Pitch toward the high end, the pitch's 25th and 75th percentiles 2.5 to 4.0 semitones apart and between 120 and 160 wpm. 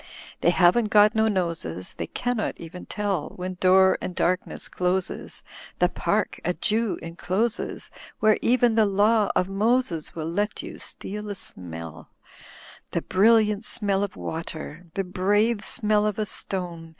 Yes: high, 195 Hz; average, 3.3 semitones; average, 150 wpm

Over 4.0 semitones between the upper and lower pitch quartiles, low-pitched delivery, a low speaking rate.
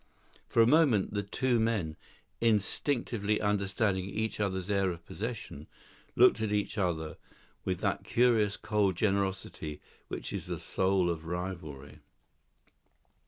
No: average, 3.2 semitones; low, 100 Hz; slow, 125 wpm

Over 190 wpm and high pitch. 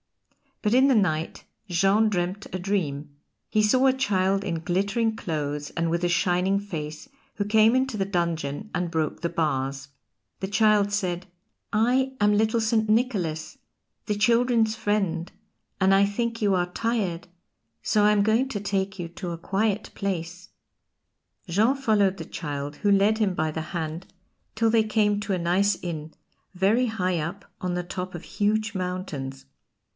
No: average, 165 wpm; high, 195 Hz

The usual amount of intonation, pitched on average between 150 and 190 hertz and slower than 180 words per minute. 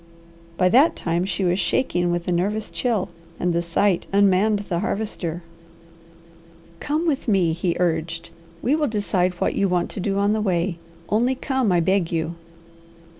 Yes: average, 3.6 semitones; medium, 185 Hz; average, 170 wpm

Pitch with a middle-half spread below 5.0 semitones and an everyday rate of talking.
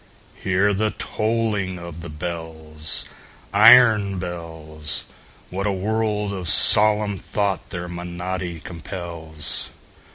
No: average, 3.6 semitones; slow, 90 wpm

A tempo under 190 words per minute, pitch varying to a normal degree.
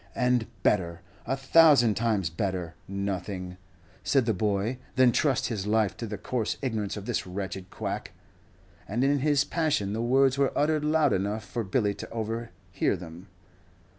Yes: average, 160 wpm; average, 5.0 semitones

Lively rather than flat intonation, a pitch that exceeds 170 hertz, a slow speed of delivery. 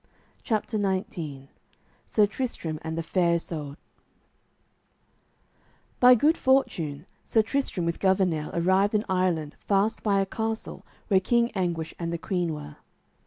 No: average, 4.6 semitones; medium, 185 Hz; slow, 130 wpm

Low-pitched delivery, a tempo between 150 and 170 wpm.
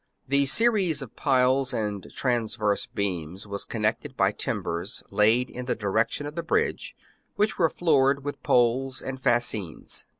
Yes: low, 125 Hz; average, 155 wpm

